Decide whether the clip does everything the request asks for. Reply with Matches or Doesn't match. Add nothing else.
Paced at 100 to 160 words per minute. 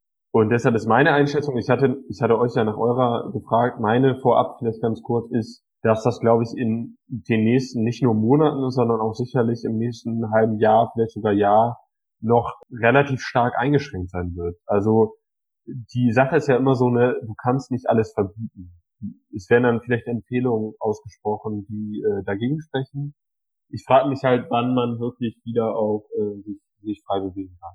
Doesn't match